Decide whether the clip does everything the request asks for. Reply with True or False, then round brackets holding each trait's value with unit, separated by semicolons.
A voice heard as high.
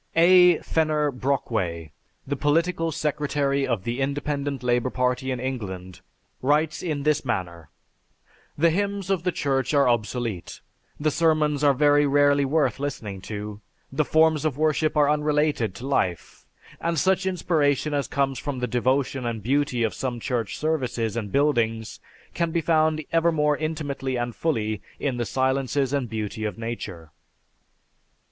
False (140 Hz)